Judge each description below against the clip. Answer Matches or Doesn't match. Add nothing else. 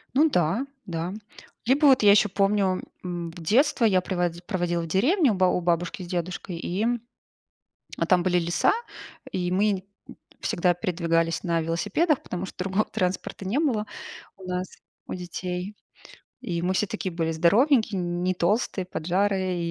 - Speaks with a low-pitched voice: Doesn't match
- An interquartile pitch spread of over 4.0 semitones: Doesn't match